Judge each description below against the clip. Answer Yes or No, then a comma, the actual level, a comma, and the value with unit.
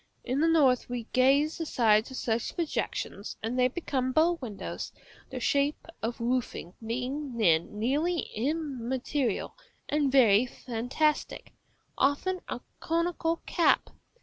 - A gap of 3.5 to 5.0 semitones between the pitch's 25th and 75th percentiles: Yes, average, 4.5 semitones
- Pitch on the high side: Yes, very high, 260 Hz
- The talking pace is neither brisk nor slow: No, slow, 125 wpm